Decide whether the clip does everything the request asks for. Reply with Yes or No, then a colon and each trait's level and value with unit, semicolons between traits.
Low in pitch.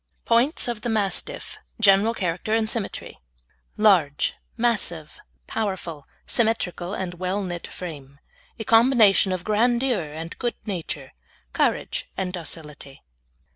No: high, 195 Hz